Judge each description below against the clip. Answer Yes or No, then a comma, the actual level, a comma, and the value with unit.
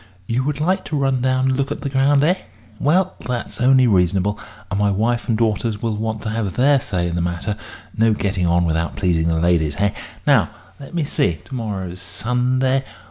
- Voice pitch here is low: Yes, low, 115 Hz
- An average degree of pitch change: No, wide, 6.1 semitones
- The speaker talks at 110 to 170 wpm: No, fast, 205 wpm